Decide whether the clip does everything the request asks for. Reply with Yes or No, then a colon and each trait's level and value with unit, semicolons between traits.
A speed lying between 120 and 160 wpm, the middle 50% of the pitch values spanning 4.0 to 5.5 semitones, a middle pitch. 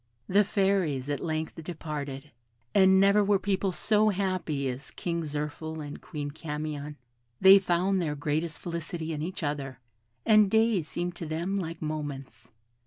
Yes: average, 150 wpm; average, 4.3 semitones; medium, 165 Hz